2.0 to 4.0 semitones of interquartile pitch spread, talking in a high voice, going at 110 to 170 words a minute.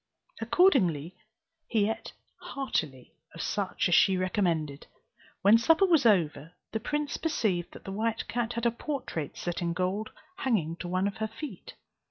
No: average, 5.2 semitones; high, 200 Hz; average, 160 wpm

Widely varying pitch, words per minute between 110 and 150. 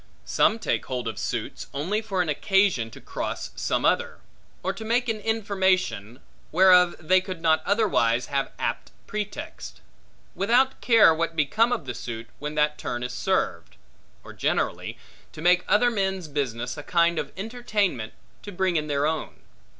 No: wide, 6.5 semitones; average, 165 wpm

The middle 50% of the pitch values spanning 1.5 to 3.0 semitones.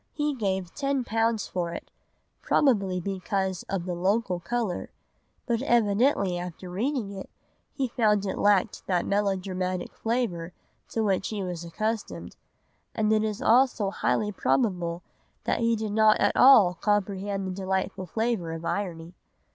No: average, 3.5 semitones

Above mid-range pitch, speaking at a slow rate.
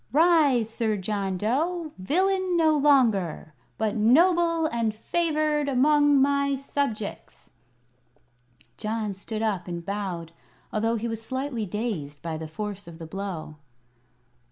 Yes: high, 225 Hz; slow, 125 wpm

